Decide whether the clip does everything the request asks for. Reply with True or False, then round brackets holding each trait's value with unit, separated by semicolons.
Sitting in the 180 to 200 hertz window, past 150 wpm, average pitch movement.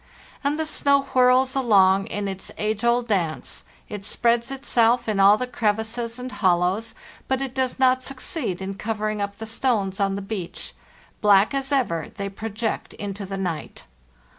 False (220 Hz; 165 wpm; 4.2 semitones)